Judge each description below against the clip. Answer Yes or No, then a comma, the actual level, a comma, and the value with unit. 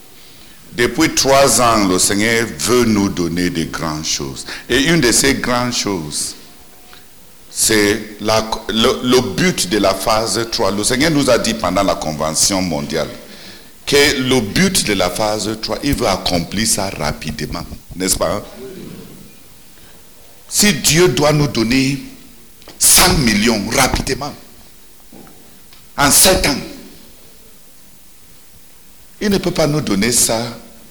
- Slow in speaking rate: Yes, slow, 130 wpm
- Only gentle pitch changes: No, wide, 5.5 semitones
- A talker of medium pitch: No, low, 110 Hz